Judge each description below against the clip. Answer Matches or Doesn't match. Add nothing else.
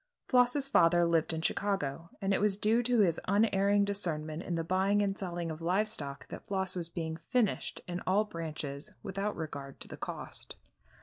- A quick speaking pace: Doesn't match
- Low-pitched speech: Doesn't match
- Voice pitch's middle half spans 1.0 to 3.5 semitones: Doesn't match